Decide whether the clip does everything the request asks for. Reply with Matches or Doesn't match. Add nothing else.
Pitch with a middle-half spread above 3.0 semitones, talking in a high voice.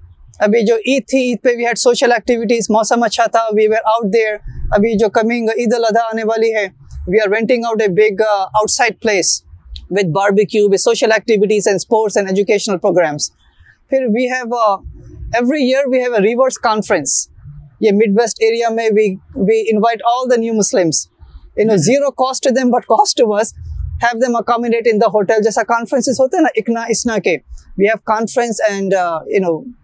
Doesn't match